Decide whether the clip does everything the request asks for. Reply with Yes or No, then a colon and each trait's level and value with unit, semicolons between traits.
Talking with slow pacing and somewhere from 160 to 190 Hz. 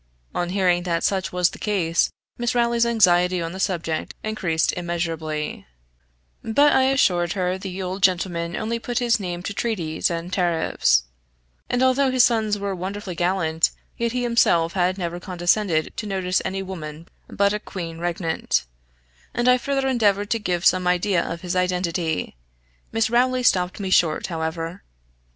No: average, 160 wpm; medium, 185 Hz